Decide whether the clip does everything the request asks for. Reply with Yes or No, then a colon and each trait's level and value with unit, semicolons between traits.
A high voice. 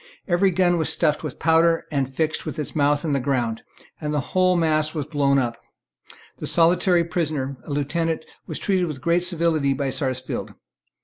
No: medium, 155 Hz